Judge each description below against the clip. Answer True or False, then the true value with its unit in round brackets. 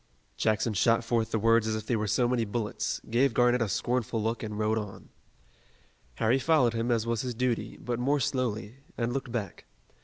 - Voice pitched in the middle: False (115 Hz)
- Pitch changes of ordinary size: False (2.1 semitones)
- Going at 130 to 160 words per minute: False (195 wpm)